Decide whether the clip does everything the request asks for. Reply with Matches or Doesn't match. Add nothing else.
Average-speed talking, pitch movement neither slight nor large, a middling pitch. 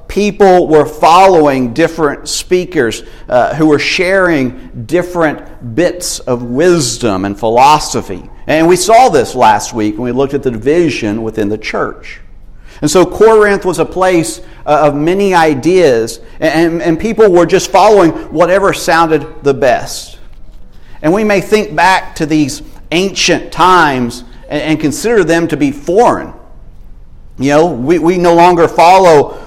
Doesn't match